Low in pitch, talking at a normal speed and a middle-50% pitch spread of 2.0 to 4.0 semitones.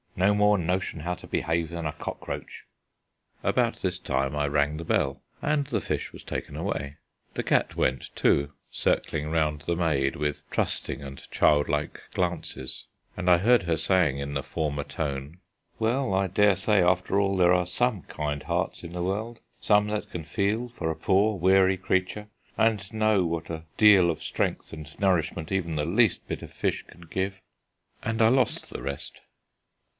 No: very low, 90 Hz; average, 180 wpm; average, 4.5 semitones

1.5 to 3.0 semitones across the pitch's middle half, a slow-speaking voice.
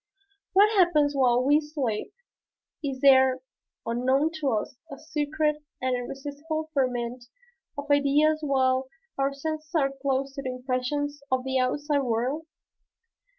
Yes: narrow, 2.6 semitones; slow, 130 wpm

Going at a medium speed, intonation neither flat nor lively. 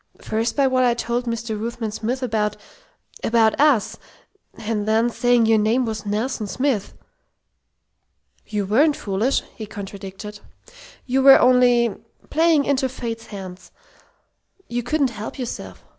No: slow, 130 wpm; average, 3.1 semitones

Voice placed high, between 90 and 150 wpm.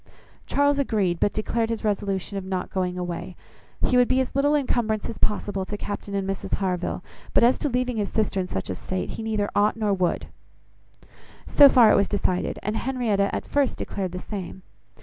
No: high, 205 Hz; average, 200 wpm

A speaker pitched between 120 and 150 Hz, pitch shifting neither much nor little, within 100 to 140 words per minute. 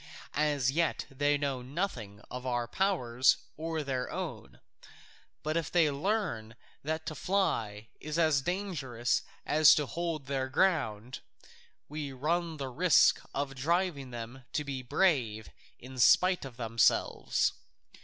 Yes: medium, 140 Hz; average, 4.5 semitones; slow, 135 wpm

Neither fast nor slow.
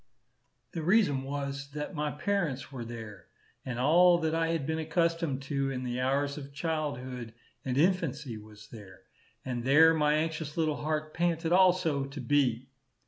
Yes: average, 160 wpm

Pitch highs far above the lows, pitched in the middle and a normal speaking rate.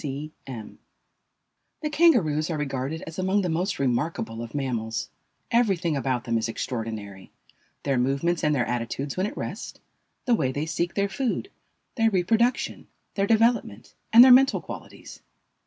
Yes: wide, 7.9 semitones; medium, 155 Hz; average, 155 wpm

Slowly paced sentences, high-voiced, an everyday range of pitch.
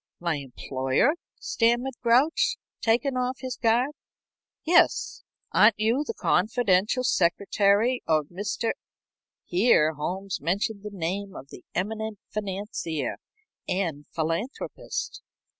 No: slow, 110 wpm; high, 205 Hz; wide, 5.7 semitones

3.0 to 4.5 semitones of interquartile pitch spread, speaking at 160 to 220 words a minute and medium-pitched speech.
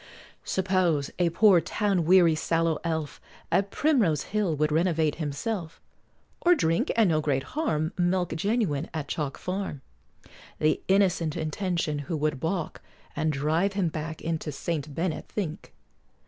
No: average, 3.5 semitones; average, 140 wpm; medium, 165 Hz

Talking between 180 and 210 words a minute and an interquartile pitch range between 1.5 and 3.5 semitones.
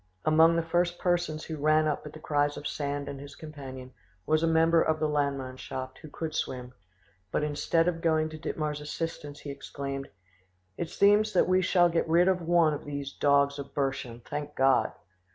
Yes: average, 190 wpm; average, 2.7 semitones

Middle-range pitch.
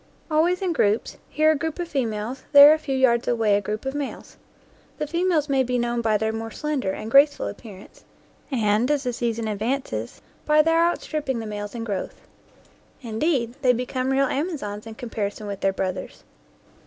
No: high, 245 Hz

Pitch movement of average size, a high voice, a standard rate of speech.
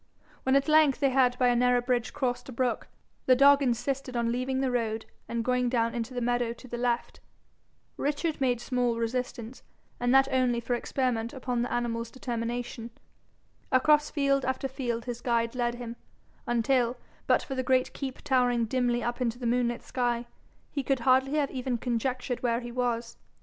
No: narrow, 1.7 semitones; high, 245 Hz; average, 180 wpm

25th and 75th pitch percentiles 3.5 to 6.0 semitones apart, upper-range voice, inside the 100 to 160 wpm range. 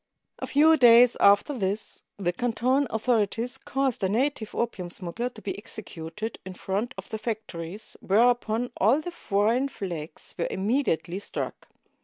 Yes: average, 4.2 semitones; high, 220 Hz; average, 150 wpm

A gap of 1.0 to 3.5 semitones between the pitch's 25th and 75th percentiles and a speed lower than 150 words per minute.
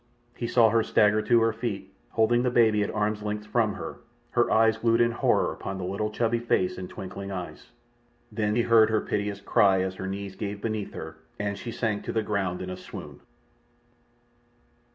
No: narrow, 2.5 semitones; average, 195 wpm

